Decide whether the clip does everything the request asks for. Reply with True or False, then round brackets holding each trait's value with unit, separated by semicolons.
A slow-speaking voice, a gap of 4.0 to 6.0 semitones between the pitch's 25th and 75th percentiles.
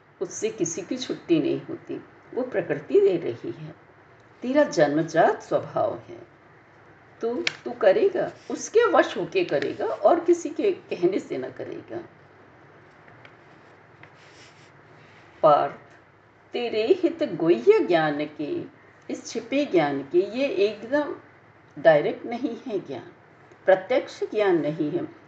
True (90 wpm; 4.7 semitones)